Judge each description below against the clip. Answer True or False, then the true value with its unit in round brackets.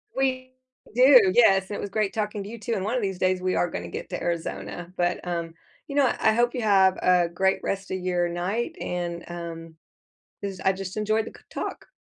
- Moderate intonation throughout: True (3.7 semitones)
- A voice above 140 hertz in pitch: True (190 Hz)